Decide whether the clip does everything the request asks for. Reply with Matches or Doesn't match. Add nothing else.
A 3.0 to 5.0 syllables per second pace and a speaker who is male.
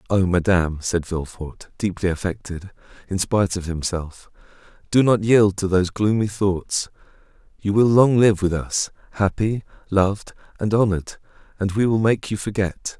Matches